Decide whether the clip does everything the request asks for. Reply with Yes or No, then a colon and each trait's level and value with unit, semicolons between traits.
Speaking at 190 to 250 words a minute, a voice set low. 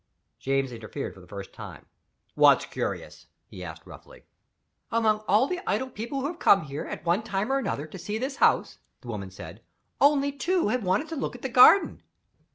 No: average, 195 wpm; high, 215 Hz